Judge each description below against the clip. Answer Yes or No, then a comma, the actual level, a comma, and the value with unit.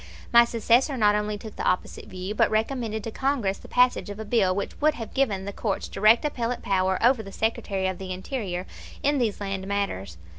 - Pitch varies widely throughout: No, average, 3.5 semitones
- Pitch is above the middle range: Yes, high, 210 Hz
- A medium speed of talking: No, fast, 210 wpm